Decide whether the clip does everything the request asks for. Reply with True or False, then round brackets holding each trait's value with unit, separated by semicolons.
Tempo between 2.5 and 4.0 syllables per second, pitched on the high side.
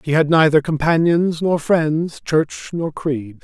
False (3.7 syllables/s; 155 Hz)